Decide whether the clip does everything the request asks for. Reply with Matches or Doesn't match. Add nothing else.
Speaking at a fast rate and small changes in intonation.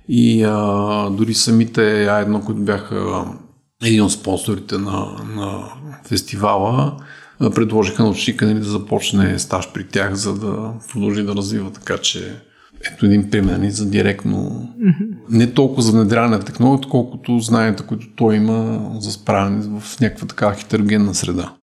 Doesn't match